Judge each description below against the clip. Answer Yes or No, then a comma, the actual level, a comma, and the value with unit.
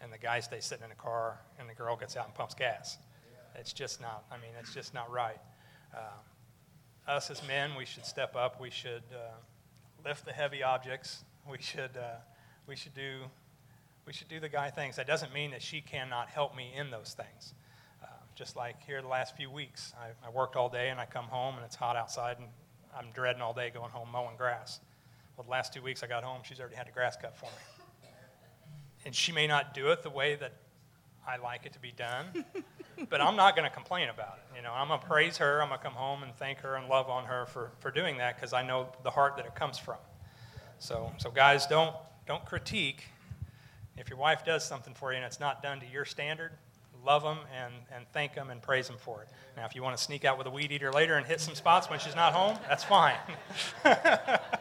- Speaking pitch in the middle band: No, low, 130 Hz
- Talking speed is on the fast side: Yes, fast, 240 wpm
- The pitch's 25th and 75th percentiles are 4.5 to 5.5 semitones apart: No, average, 2.9 semitones